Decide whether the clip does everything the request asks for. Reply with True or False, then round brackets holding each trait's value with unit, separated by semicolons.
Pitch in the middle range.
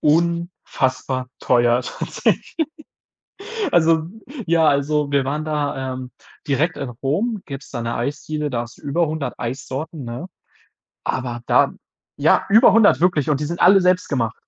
True (145 Hz)